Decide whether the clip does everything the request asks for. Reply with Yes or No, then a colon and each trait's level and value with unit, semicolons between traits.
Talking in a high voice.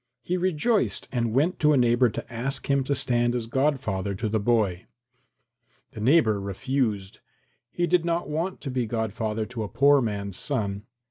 No: low, 120 Hz